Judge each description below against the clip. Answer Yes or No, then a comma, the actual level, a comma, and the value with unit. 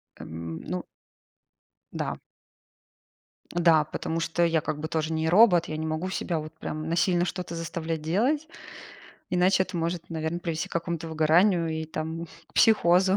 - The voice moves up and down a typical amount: No, narrow, 1.9 semitones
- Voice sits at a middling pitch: Yes, medium, 165 Hz